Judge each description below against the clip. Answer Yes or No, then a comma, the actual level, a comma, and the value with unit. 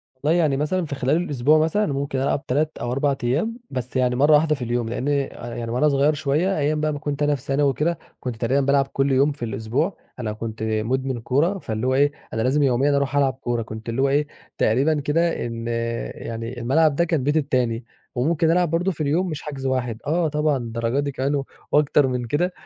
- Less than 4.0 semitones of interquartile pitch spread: Yes, average, 3.5 semitones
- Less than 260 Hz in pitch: Yes, medium, 140 Hz